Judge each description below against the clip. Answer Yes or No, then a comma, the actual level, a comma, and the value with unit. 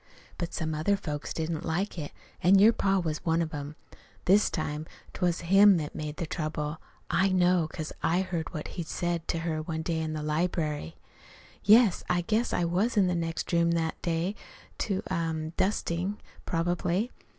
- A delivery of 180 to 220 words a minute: Yes, average, 185 wpm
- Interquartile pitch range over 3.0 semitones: No, average, 2.7 semitones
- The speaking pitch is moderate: Yes, medium, 170 Hz